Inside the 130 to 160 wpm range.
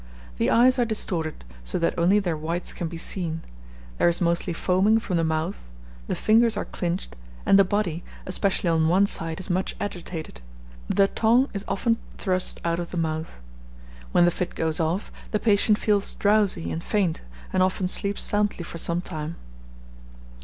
No: average, 175 wpm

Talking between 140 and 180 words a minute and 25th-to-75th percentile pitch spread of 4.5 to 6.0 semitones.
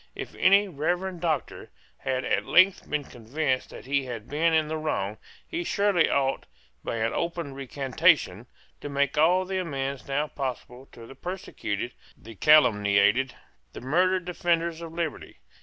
Yes: average, 155 wpm; average, 4.9 semitones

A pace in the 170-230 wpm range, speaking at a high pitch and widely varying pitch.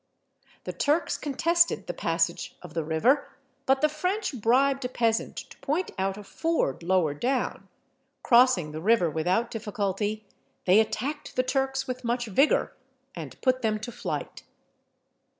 No: average, 150 wpm; high, 240 Hz; wide, 5.7 semitones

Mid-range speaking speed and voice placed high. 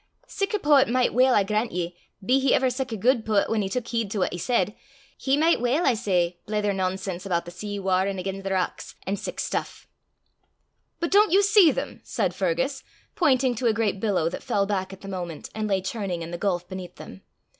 No: fast, 225 wpm; high, 210 Hz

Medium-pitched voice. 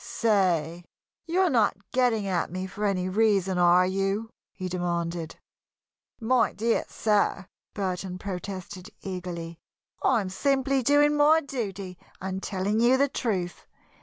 No: high, 195 Hz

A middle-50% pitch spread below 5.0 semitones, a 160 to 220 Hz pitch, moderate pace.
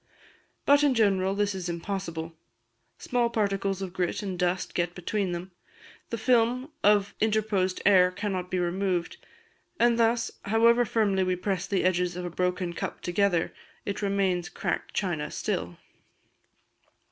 Yes: average, 2.8 semitones; high, 190 Hz; average, 145 wpm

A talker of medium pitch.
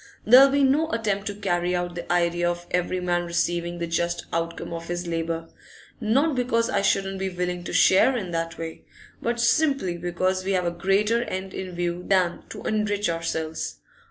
Yes: medium, 180 Hz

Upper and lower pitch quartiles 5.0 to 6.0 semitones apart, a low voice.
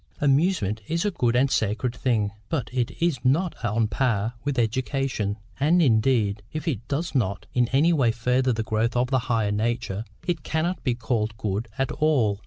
No: average, 4.2 semitones; low, 125 Hz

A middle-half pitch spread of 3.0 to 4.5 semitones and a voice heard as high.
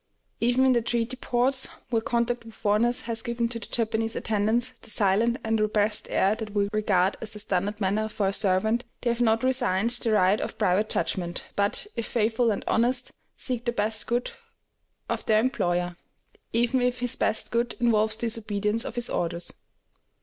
No: narrow, 2.4 semitones; high, 225 Hz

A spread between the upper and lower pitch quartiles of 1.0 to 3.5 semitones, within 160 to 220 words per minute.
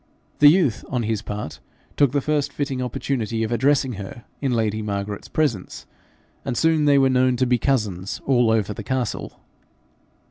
No: average, 4.2 semitones; average, 170 wpm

